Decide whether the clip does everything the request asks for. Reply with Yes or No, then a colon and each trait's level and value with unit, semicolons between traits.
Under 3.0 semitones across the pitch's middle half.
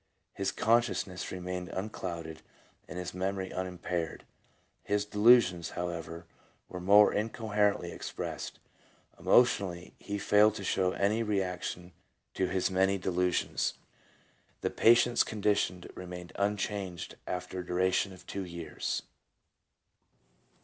Yes: narrow, 2.5 semitones